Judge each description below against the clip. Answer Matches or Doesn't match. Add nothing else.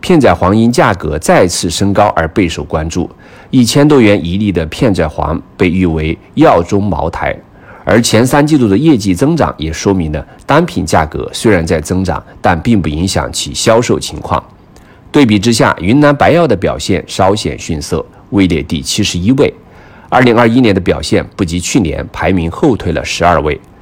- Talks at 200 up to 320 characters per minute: Matches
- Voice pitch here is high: Doesn't match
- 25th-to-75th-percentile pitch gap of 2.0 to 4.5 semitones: Doesn't match